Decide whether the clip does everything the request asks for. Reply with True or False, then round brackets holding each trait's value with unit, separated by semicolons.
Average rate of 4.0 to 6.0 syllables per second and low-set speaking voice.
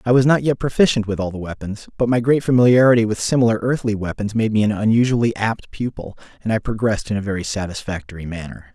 False (6.6 syllables/s; 110 Hz)